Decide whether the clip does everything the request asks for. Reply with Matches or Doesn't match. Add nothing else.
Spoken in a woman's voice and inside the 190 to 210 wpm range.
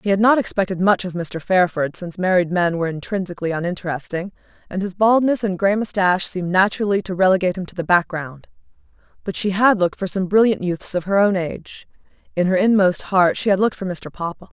Matches